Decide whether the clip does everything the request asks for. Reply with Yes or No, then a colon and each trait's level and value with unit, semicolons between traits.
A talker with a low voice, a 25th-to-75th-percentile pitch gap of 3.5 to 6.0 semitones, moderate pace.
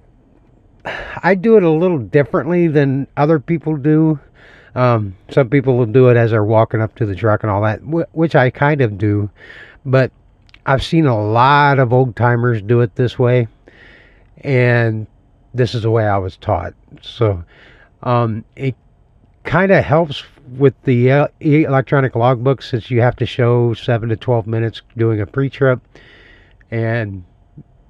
Yes: low, 120 Hz; average, 3.8 semitones; average, 160 wpm